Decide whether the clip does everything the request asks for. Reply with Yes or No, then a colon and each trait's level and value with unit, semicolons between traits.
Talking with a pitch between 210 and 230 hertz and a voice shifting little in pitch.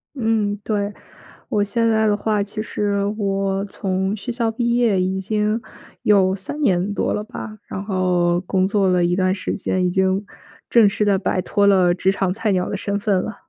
No: high, 200 Hz; narrow, 2.1 semitones